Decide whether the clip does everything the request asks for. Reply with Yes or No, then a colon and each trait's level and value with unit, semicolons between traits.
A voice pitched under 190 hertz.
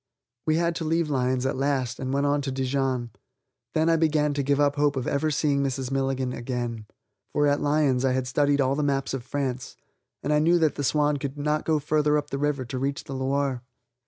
Yes: medium, 140 Hz